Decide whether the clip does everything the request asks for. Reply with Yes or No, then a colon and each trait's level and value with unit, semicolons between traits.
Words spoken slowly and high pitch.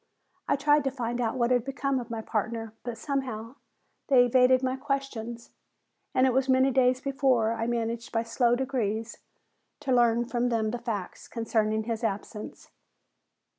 No: average, 165 wpm; high, 240 Hz